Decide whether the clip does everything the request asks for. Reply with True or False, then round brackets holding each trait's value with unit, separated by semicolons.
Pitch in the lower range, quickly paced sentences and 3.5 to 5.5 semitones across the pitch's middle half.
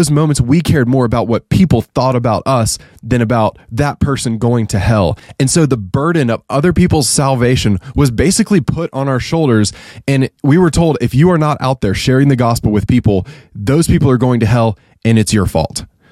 True (130 Hz; 210 wpm; 4.4 semitones)